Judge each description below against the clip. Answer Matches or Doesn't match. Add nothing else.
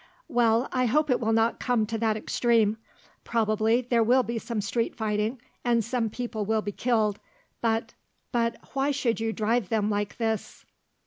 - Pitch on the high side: Matches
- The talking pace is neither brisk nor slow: Matches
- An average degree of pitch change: Doesn't match